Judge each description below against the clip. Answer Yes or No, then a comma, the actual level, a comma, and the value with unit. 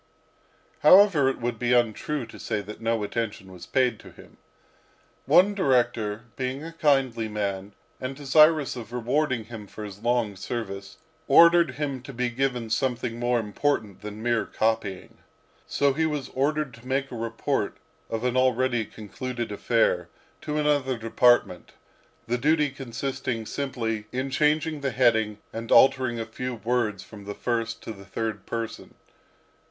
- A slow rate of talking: No, average, 155 wpm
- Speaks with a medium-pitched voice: No, low, 120 Hz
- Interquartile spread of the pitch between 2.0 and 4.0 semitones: Yes, average, 3.4 semitones